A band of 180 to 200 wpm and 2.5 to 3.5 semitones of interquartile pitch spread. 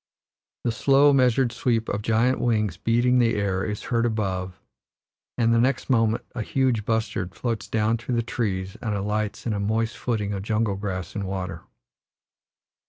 No: average, 170 wpm; average, 2.8 semitones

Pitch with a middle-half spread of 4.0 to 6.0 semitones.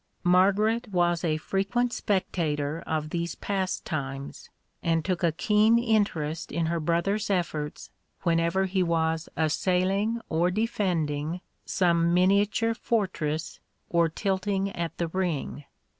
No: average, 3.4 semitones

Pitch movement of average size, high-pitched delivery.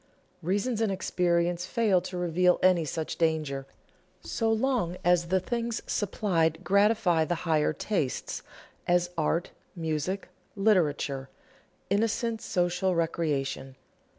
No: average, 3.7 semitones; medium, 175 Hz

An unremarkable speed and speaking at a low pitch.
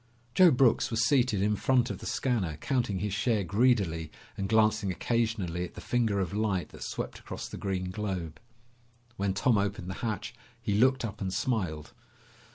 Yes: average, 175 wpm; low, 105 Hz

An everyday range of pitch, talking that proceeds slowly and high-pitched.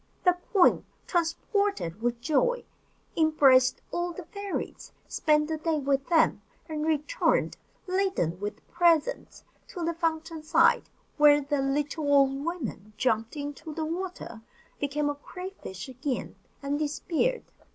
Yes: average, 3.9 semitones; slow, 130 wpm; very high, 305 Hz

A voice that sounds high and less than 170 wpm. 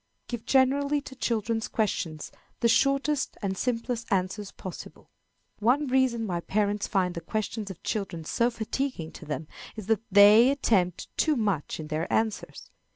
Yes: high, 220 Hz; average, 155 wpm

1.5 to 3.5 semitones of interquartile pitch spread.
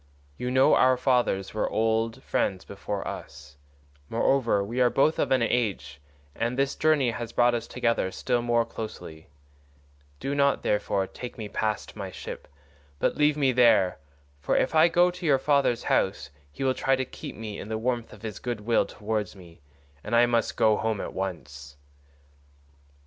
No: average, 4.0 semitones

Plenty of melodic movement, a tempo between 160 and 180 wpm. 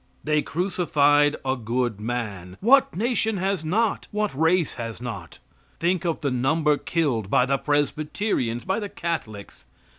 No: wide, 6.8 semitones; average, 145 wpm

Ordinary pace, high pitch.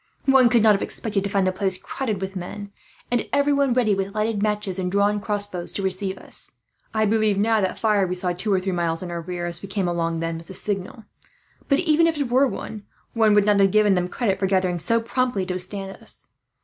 No: fast, 235 wpm; high, 200 Hz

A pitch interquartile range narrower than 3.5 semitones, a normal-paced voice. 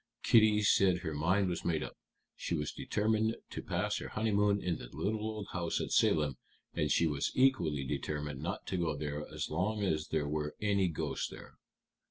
No: wide, 5.4 semitones; average, 190 wpm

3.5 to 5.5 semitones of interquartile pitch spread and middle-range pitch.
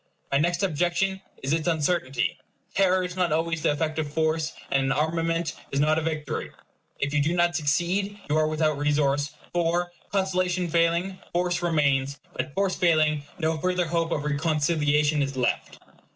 No: average, 2.9 semitones; medium, 160 Hz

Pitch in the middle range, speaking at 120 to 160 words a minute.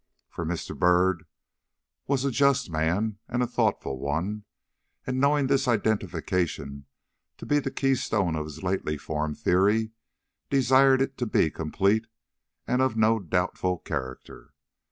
No: low, 100 Hz; average, 140 wpm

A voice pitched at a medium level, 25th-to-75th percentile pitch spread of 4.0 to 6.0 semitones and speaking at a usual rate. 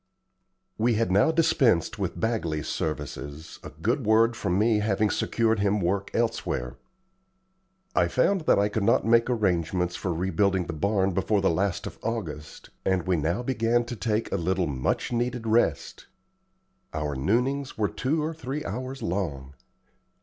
No: low, 105 Hz; average, 5.1 semitones; average, 155 wpm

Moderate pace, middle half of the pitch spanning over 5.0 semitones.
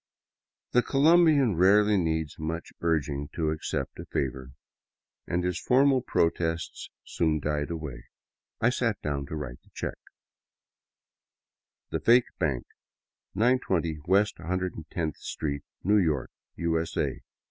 No: slow, 125 wpm; wide, 5.4 semitones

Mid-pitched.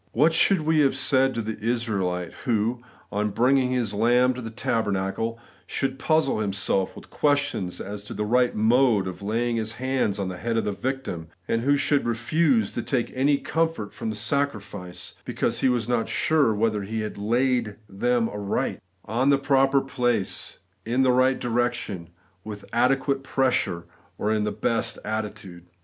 No: low, 115 Hz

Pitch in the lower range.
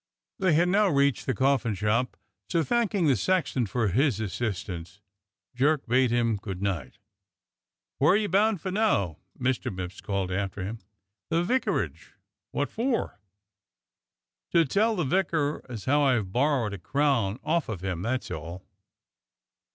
Yes: low, 130 Hz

